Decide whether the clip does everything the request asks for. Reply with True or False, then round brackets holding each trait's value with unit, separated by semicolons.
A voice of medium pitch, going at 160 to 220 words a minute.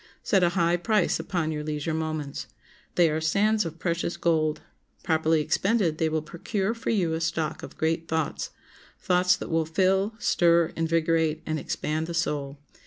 True (165 Hz; 165 wpm)